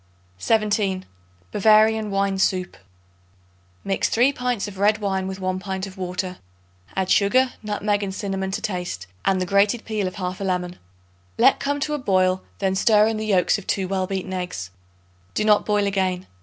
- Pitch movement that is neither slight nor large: No, narrow, 2.2 semitones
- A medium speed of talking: Yes, average, 180 wpm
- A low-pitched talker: No, high, 195 Hz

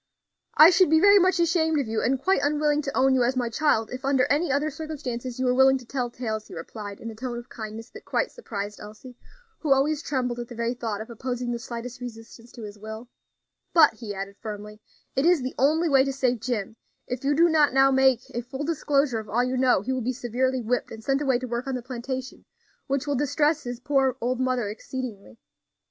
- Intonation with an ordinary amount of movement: Yes, average, 3.1 semitones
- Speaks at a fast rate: Yes, fast, 230 wpm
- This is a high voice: Yes, very high, 255 Hz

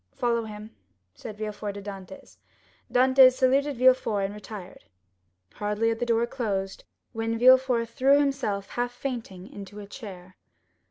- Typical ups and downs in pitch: Yes, average, 3.9 semitones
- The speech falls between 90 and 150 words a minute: Yes, average, 140 wpm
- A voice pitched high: Yes, high, 225 Hz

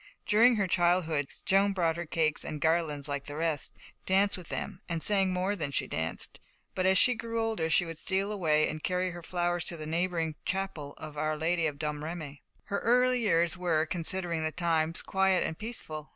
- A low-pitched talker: No, medium, 170 Hz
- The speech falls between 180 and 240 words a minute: Yes, average, 195 wpm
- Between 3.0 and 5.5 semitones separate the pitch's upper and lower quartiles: Yes, average, 3.4 semitones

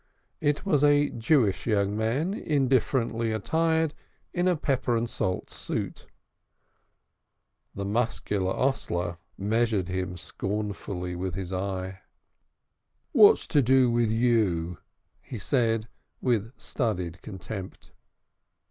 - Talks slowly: Yes, slow, 105 wpm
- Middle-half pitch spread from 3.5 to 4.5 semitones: No, wide, 5.6 semitones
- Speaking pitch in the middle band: No, low, 110 Hz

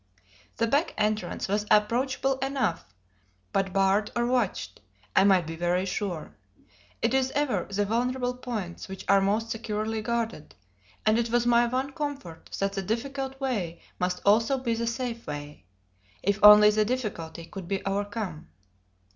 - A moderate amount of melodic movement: Yes, average, 4.0 semitones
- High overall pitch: Yes, high, 215 Hz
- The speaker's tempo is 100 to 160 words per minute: Yes, average, 155 wpm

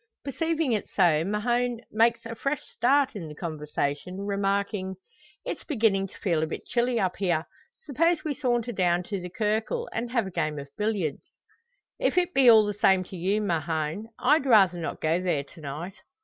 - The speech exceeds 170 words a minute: Yes, average, 185 wpm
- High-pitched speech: Yes, high, 200 Hz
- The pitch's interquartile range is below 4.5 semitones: No, wide, 5.6 semitones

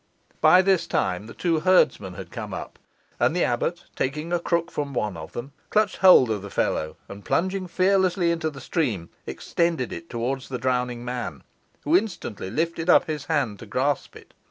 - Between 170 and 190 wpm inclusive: Yes, average, 185 wpm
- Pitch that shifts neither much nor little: No, wide, 6.5 semitones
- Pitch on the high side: No, medium, 145 Hz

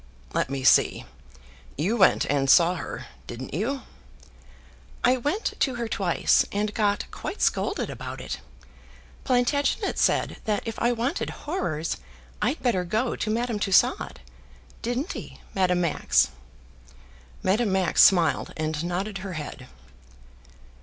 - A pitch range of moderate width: No, wide, 5.7 semitones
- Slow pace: Yes, slow, 130 wpm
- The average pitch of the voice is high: Yes, high, 205 Hz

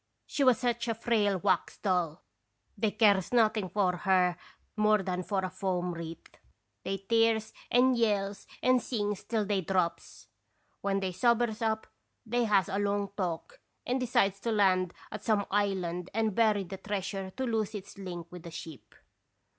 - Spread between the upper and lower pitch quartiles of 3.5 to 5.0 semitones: No, average, 3.1 semitones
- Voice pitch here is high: Yes, high, 200 Hz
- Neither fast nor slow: Yes, average, 170 wpm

